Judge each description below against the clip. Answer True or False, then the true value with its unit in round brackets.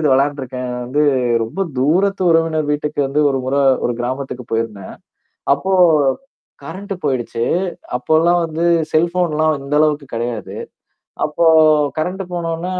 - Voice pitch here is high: False (150 Hz)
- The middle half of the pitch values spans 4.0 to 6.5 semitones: True (4.3 semitones)